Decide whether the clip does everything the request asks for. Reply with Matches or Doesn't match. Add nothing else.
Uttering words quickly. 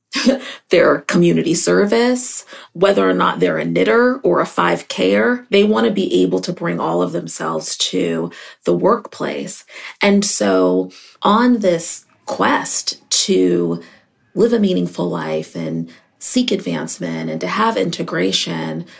Doesn't match